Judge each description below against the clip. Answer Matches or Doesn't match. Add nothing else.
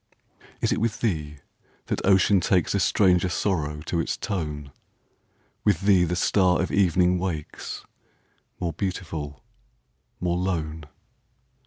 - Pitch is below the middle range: Matches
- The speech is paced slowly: Matches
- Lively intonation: Doesn't match